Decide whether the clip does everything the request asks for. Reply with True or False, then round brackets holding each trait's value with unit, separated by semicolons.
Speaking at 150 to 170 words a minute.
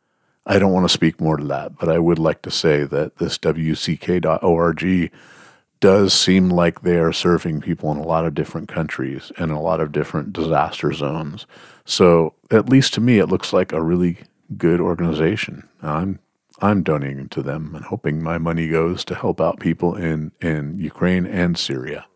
False (185 wpm)